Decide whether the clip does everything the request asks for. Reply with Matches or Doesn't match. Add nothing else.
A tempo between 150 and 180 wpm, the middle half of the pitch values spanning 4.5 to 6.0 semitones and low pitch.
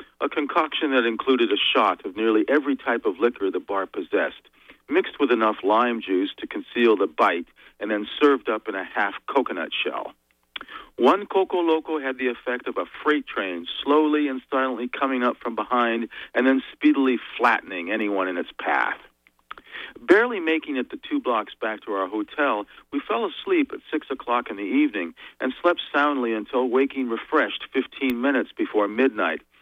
Matches